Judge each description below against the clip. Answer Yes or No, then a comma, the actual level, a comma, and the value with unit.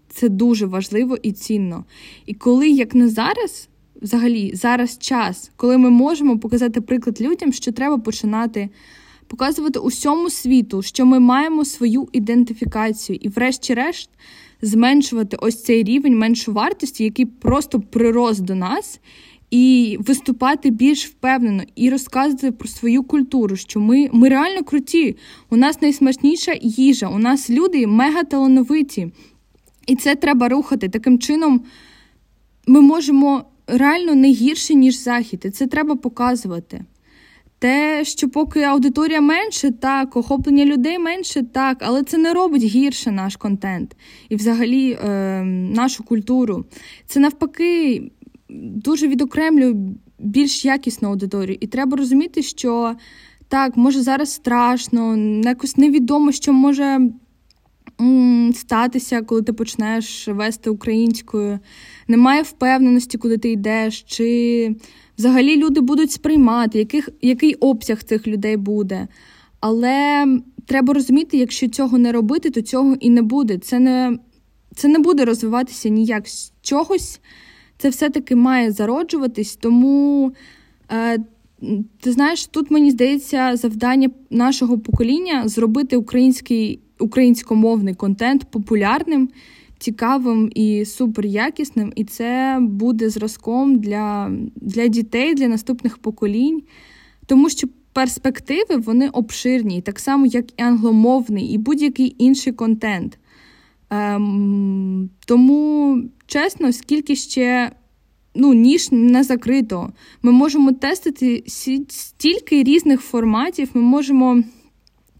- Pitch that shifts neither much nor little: Yes, average, 3.4 semitones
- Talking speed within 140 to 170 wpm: No, average, 120 wpm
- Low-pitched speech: No, very high, 250 Hz